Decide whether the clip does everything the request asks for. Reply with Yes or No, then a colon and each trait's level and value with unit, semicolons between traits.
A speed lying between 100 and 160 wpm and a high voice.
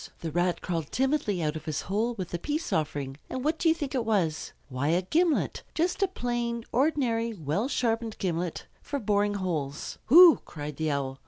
No: average, 190 wpm; high, 205 Hz